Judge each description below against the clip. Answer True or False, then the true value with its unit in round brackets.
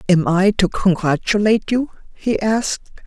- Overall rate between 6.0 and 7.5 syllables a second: False (4.7 syllables/s)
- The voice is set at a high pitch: True (200 Hz)